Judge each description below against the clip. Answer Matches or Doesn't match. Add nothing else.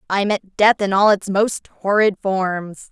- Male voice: Doesn't match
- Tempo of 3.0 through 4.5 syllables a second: Matches